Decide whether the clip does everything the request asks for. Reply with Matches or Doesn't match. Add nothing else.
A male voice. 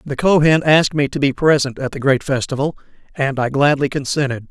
Matches